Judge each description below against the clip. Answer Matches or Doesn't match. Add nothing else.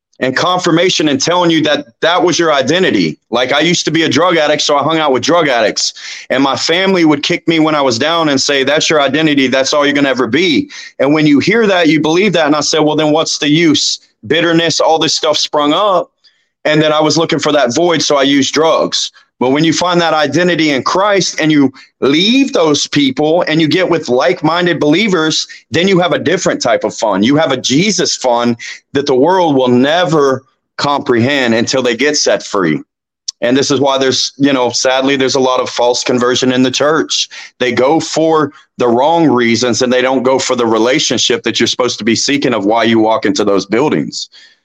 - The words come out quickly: Matches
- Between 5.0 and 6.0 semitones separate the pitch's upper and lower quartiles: Doesn't match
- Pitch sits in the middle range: Matches